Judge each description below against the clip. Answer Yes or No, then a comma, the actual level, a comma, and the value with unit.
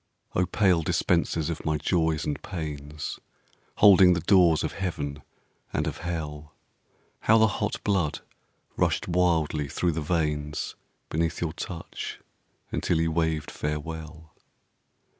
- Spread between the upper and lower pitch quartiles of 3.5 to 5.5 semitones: No, average, 2.7 semitones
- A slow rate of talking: Yes, slow, 125 wpm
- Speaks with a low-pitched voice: Yes, very low, 80 Hz